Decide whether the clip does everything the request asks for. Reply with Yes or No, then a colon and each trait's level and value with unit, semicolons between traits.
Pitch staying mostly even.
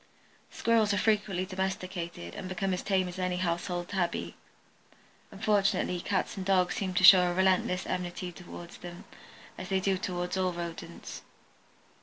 Yes: narrow, 1.5 semitones